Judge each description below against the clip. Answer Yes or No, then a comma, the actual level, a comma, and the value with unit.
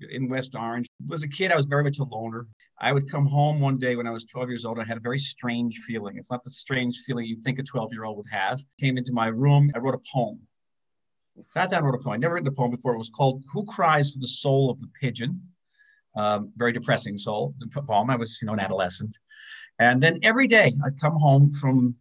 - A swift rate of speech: Yes, fast, 265 wpm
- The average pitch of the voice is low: Yes, low, 130 Hz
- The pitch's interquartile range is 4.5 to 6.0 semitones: No, average, 3.3 semitones